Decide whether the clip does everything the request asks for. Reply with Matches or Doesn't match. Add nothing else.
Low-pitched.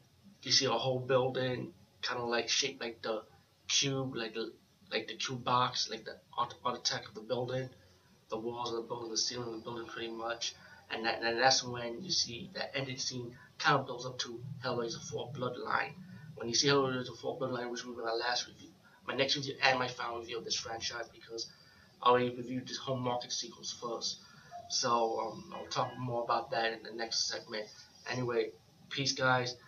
Matches